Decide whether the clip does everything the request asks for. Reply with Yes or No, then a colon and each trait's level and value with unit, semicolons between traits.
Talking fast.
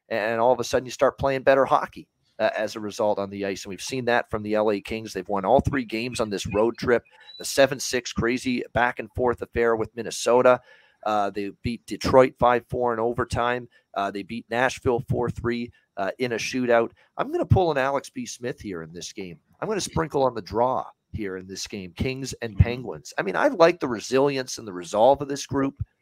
Yes: fast, 230 wpm